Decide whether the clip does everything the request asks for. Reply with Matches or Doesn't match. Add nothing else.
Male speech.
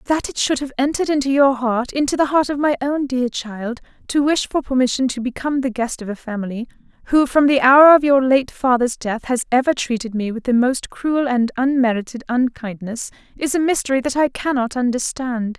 Doesn't match